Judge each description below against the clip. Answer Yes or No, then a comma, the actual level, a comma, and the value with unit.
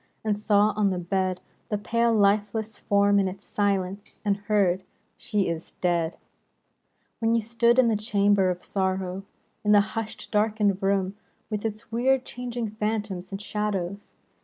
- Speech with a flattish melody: Yes, narrow, 2.0 semitones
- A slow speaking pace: No, average, 160 wpm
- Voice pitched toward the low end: No, high, 205 Hz